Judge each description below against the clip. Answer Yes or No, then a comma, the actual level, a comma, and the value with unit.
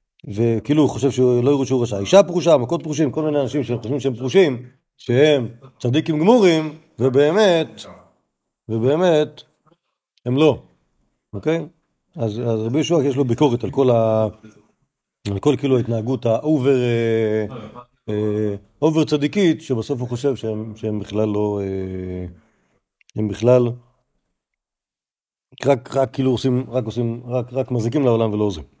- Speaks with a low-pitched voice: Yes, low, 125 Hz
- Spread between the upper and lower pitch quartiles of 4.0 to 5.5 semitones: Yes, average, 4.8 semitones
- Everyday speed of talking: Yes, average, 140 wpm